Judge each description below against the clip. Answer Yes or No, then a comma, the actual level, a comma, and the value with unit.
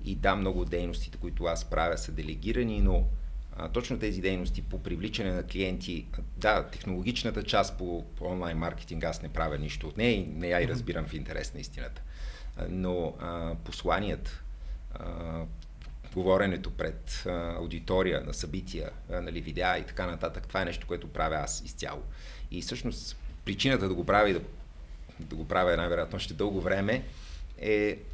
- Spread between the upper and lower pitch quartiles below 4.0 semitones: Yes, average, 3.1 semitones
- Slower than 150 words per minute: No, fast, 165 wpm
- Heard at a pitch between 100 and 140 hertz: No, very low, 85 Hz